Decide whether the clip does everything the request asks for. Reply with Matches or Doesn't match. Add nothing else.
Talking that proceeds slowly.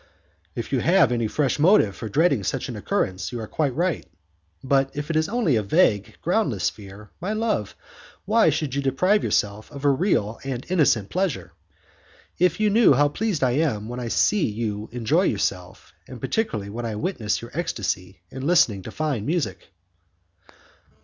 Doesn't match